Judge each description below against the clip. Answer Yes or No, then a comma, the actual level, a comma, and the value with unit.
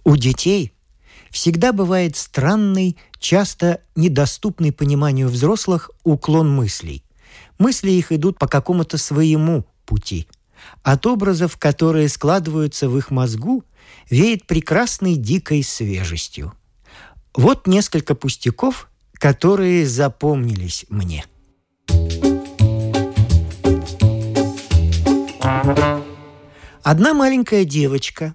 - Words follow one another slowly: Yes, slow, 80 wpm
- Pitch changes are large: Yes, wide, 7.8 semitones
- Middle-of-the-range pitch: Yes, medium, 145 Hz